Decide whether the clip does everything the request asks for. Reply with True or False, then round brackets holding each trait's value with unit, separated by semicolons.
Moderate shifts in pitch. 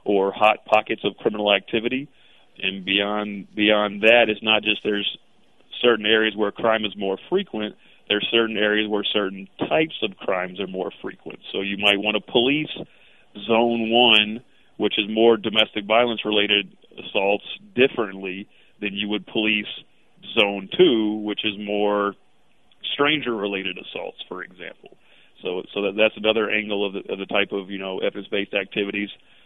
False (1.5 semitones)